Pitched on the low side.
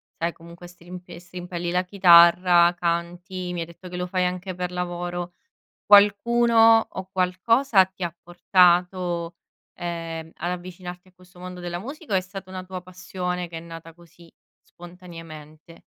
No: medium, 180 Hz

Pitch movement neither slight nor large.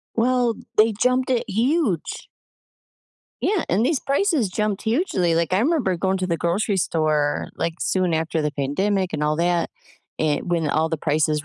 No: wide, 6.2 semitones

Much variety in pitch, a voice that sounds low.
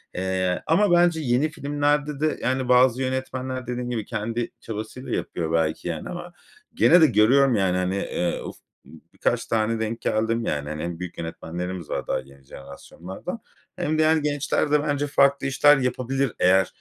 Yes: wide, 7.6 semitones; low, 125 Hz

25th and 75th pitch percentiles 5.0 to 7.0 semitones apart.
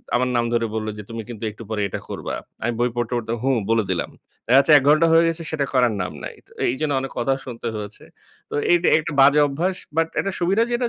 Yes: wide, 5.6 semitones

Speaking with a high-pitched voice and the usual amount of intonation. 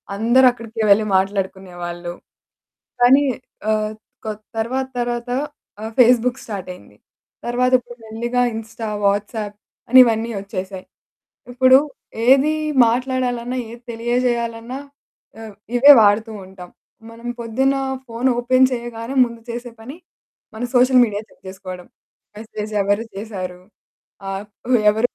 Yes: high, 230 Hz; average, 3.1 semitones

